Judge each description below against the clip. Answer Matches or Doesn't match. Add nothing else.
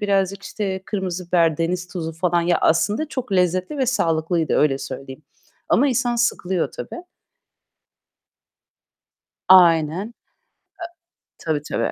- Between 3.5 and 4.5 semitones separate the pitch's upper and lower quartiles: Matches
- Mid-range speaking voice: Matches